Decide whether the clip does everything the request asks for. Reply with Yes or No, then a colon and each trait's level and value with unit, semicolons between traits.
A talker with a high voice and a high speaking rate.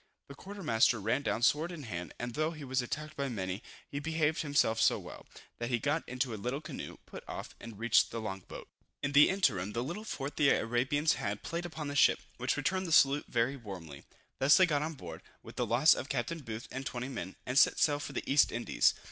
No: low, 135 Hz; fast, 230 wpm